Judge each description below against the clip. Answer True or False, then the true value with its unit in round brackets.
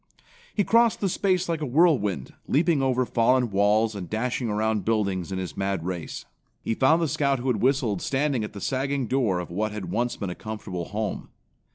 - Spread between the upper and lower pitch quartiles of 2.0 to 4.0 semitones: False (5.3 semitones)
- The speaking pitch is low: True (115 Hz)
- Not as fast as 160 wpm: False (200 wpm)